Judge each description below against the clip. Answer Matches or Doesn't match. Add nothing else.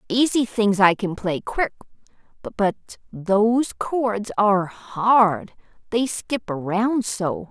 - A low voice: Doesn't match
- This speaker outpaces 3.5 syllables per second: Doesn't match